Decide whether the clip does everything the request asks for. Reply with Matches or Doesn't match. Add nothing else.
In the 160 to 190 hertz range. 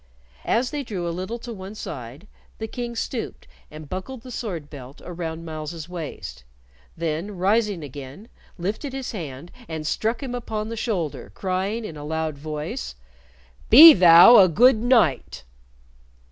Matches